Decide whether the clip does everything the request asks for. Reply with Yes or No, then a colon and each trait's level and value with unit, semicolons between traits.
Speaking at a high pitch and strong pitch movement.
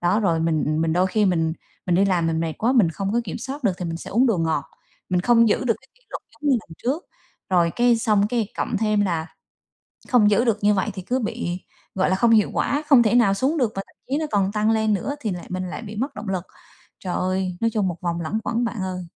No: high, 205 Hz; average, 4.6 semitones